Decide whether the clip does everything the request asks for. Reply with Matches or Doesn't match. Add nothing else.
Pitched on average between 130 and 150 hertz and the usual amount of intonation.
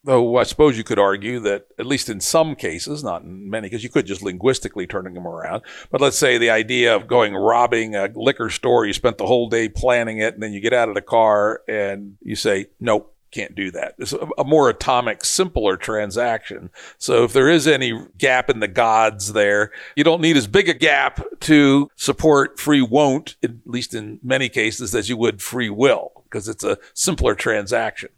Doesn't match